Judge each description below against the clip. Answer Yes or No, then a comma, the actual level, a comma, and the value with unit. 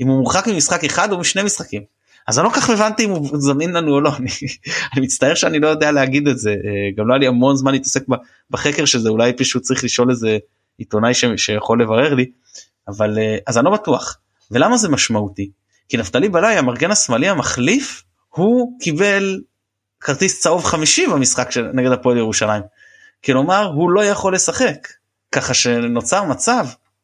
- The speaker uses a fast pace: Yes, fast, 175 wpm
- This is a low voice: Yes, low, 130 Hz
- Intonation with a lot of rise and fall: Yes, wide, 6.0 semitones